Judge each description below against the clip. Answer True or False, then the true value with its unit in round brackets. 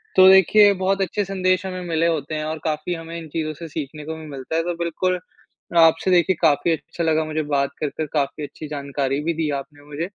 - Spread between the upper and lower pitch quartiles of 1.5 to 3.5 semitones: True (2.9 semitones)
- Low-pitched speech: False (160 Hz)